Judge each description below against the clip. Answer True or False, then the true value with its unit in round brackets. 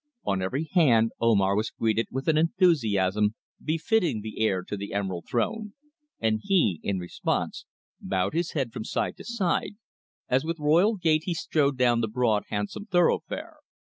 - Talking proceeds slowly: False (165 wpm)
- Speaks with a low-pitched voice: True (125 Hz)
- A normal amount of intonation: False (8.2 semitones)